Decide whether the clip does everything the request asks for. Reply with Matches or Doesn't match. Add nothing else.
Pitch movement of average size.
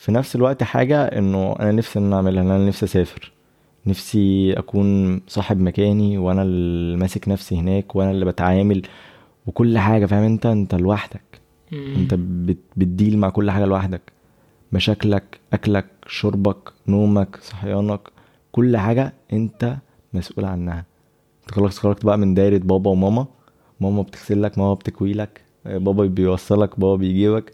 Doesn't match